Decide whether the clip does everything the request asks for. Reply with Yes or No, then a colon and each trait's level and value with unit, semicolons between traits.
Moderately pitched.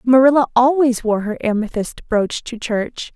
No: high, 240 Hz